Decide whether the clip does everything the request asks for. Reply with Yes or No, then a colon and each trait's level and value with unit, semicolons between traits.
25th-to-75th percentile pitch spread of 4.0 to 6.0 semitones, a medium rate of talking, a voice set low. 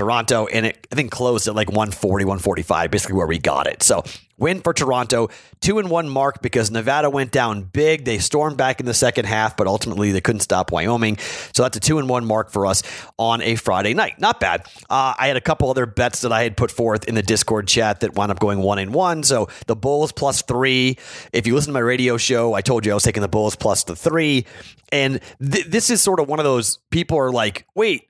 No: average, 4.3 semitones; fast, 245 wpm; low, 120 Hz